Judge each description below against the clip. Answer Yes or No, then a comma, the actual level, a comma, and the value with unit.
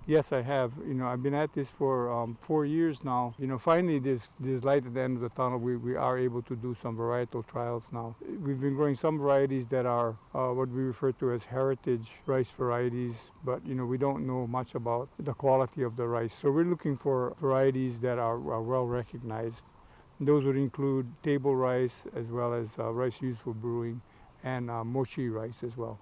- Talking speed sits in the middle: No, fast, 220 wpm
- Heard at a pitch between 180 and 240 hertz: No, low, 125 Hz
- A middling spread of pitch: No, narrow, 2.2 semitones